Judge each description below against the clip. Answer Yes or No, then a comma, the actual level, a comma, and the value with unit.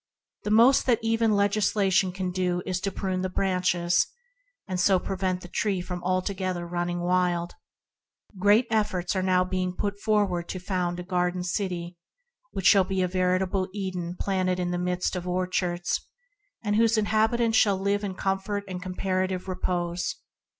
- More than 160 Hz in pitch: Yes, medium, 185 Hz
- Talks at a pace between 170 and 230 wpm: No, average, 155 wpm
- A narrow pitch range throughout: Yes, narrow, 1.9 semitones